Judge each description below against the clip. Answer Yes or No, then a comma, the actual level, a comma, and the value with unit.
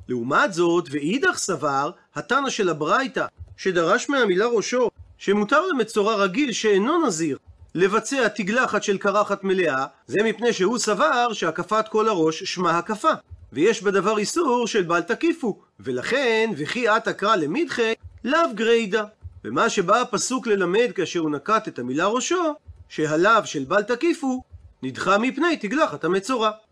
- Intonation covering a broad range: Yes, wide, 5.7 semitones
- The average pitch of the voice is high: Yes, high, 210 Hz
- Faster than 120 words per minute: Yes, average, 135 wpm